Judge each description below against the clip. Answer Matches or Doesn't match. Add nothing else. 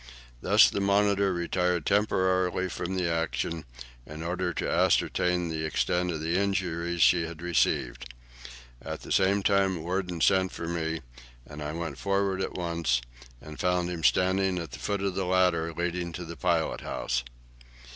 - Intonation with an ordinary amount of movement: Doesn't match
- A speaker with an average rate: Matches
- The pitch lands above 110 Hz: Doesn't match